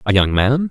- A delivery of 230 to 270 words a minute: Yes, fast, 255 wpm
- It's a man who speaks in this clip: Yes, male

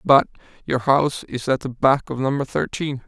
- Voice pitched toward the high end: No, low, 135 Hz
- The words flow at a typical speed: Yes, average, 175 wpm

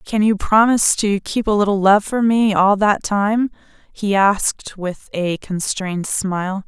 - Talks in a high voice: Yes, high, 205 Hz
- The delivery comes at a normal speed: Yes, average, 170 wpm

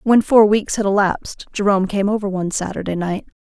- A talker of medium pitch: No, high, 200 Hz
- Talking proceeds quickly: No, average, 195 wpm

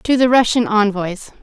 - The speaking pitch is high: Yes, high, 220 Hz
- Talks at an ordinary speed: Yes, average, 170 wpm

